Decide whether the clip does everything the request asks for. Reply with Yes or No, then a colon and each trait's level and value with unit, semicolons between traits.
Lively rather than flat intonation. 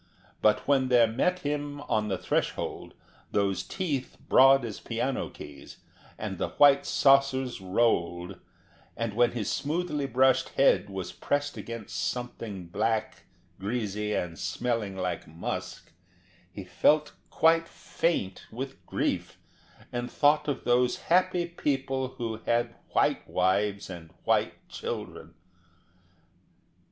Yes: wide, 5.7 semitones